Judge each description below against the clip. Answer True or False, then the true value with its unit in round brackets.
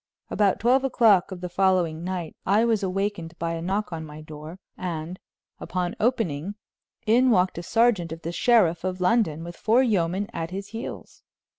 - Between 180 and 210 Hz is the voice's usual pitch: True (185 Hz)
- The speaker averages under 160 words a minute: False (175 wpm)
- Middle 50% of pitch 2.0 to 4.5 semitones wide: True (4.2 semitones)